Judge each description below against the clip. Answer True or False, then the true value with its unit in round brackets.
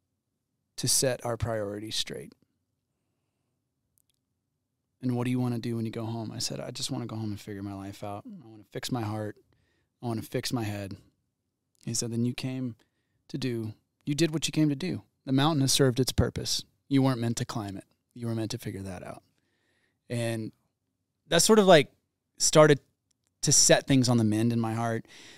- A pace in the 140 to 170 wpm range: False (200 wpm)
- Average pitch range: True (3.1 semitones)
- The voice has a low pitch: True (120 Hz)